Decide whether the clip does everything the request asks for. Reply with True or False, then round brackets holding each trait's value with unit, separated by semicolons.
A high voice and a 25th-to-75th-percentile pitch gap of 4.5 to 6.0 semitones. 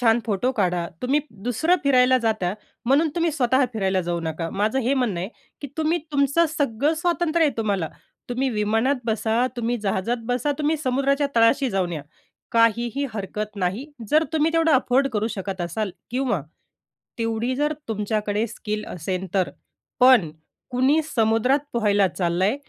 True (230 Hz; 5.3 semitones)